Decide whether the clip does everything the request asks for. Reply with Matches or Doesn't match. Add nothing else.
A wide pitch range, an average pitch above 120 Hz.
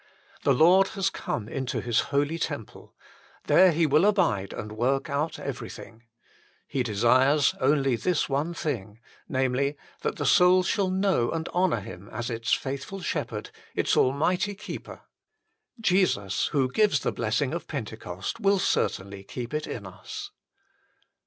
Matches